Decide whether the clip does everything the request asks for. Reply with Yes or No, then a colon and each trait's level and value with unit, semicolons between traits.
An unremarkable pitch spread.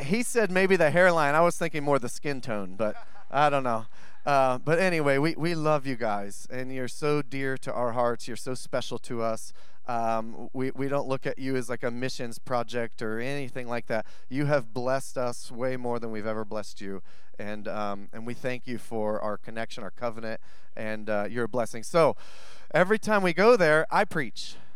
Yes: average, 3.9 semitones